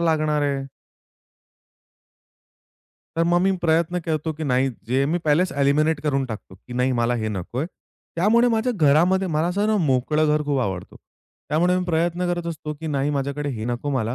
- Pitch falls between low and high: Yes, medium, 150 Hz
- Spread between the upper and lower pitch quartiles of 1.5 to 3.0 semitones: No, average, 4.0 semitones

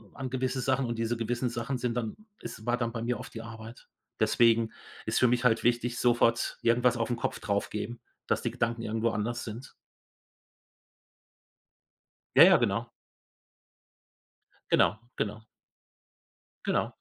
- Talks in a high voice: No, low, 115 Hz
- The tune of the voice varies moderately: No, narrow, 1.2 semitones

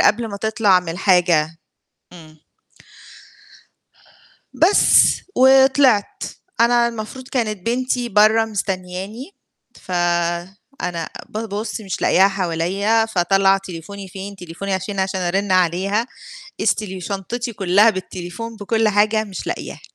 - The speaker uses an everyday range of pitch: Yes, average, 3.5 semitones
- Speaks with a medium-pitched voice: No, high, 200 Hz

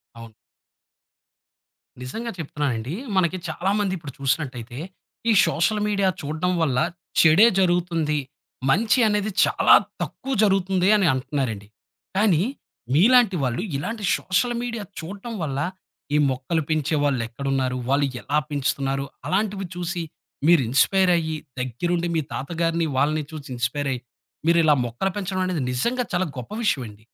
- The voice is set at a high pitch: No, medium, 160 Hz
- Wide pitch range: Yes, wide, 5.8 semitones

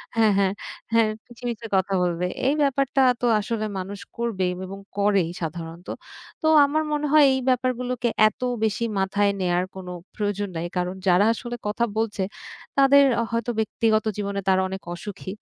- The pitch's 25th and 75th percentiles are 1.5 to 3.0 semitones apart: No, average, 4.1 semitones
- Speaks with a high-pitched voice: Yes, high, 210 Hz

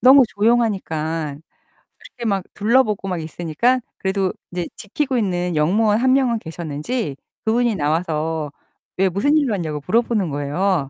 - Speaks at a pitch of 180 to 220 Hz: Yes, high, 190 Hz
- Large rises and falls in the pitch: Yes, wide, 6.4 semitones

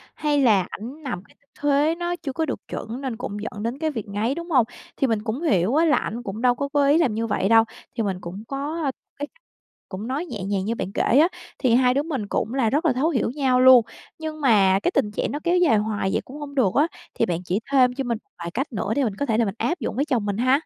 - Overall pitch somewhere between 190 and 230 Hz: No, very high, 250 Hz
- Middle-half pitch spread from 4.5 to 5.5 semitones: Yes, average, 5.1 semitones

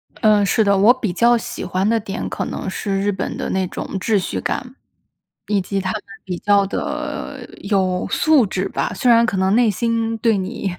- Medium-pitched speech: No, high, 205 Hz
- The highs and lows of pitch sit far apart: No, average, 3.1 semitones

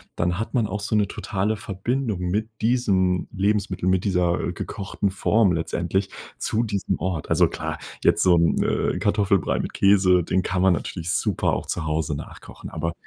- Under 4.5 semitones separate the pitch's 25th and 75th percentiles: Yes, average, 2.7 semitones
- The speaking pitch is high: No, very low, 95 Hz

